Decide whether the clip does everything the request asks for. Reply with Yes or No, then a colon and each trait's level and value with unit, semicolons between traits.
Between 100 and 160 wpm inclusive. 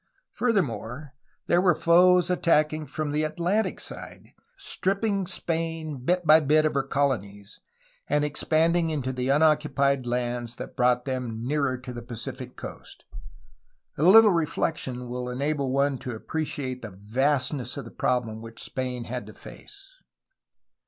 Yes: average, 140 wpm